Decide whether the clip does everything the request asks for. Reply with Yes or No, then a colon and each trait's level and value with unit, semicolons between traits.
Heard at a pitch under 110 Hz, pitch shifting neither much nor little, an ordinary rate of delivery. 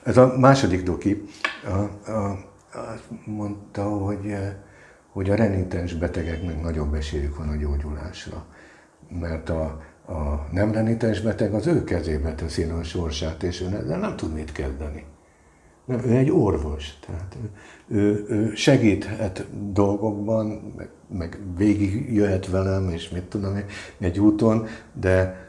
Yes: very low, 95 Hz; average, 4.4 semitones; average, 130 wpm